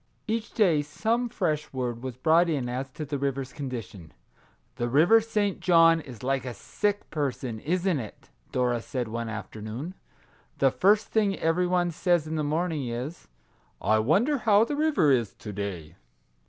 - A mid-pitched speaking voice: Yes, medium, 150 Hz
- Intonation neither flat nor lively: No, wide, 6.9 semitones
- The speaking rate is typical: Yes, average, 180 wpm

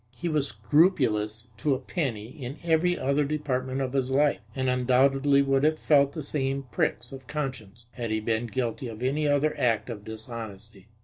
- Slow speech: No, average, 180 wpm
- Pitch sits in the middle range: No, low, 130 Hz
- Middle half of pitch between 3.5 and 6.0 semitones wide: Yes, average, 3.8 semitones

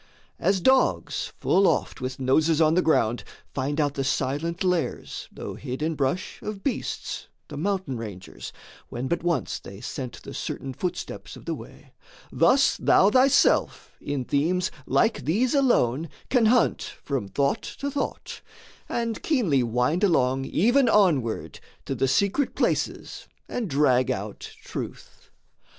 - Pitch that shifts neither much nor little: No, wide, 7.4 semitones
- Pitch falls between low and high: Yes, medium, 155 Hz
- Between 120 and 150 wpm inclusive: Yes, average, 145 wpm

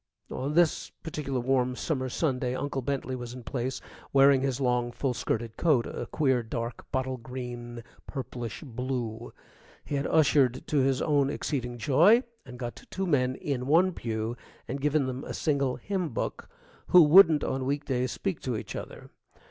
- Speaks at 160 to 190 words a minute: Yes, average, 170 wpm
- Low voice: Yes, low, 130 Hz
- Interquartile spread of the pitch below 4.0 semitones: Yes, average, 2.8 semitones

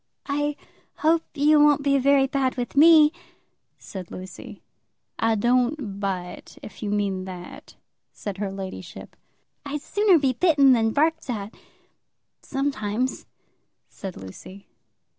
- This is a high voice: Yes, very high, 255 Hz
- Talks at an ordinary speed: No, slow, 120 wpm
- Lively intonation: Yes, wide, 6.5 semitones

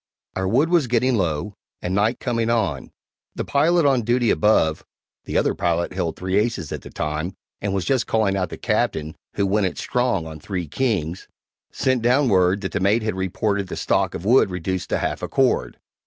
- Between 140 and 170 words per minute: No, average, 200 wpm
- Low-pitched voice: Yes, low, 100 Hz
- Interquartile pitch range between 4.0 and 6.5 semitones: Yes, average, 4.8 semitones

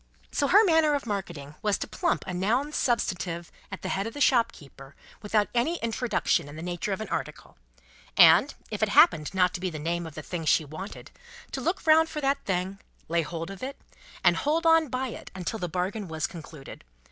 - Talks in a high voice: Yes, high, 195 Hz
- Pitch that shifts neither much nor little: No, wide, 7.7 semitones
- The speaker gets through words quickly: Yes, fast, 210 wpm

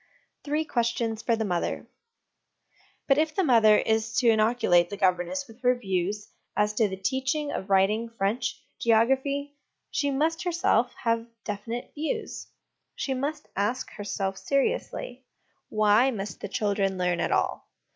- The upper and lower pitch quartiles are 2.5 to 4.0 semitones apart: No, average, 4.7 semitones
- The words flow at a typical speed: Yes, average, 145 wpm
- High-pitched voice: Yes, high, 230 Hz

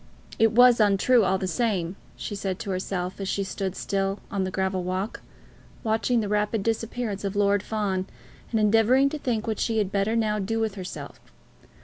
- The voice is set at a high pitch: Yes, high, 205 Hz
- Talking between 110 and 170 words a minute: No, average, 190 wpm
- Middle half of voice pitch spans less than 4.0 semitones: Yes, average, 2.7 semitones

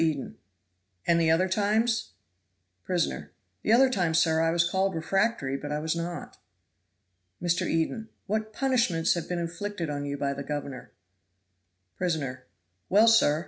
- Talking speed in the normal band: Yes, average, 145 wpm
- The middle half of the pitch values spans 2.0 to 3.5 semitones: No, average, 4.5 semitones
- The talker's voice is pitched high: No, medium, 170 Hz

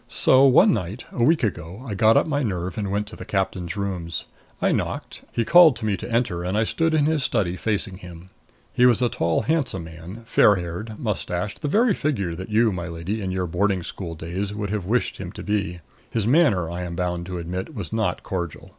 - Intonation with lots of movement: No, average, 4.7 semitones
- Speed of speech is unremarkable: No, fast, 225 wpm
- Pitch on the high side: No, low, 100 Hz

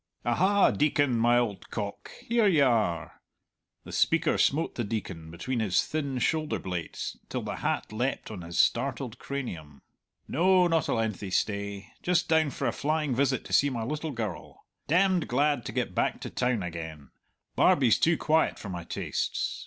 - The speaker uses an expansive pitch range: Yes, wide, 7.2 semitones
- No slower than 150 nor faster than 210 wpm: Yes, average, 170 wpm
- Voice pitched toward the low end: Yes, low, 125 Hz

